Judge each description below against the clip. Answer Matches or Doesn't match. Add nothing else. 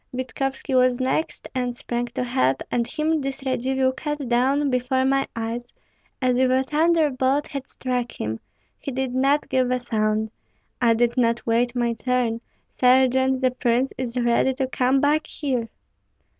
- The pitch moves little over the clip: Matches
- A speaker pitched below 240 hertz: Doesn't match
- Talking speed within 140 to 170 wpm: Matches